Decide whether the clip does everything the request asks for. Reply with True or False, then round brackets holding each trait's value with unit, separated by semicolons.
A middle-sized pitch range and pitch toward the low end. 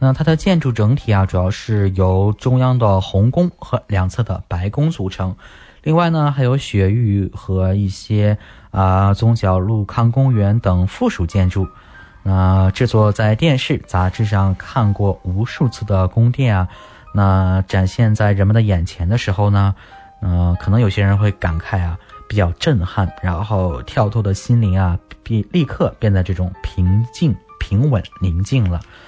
True (3.6 semitones; 100 Hz)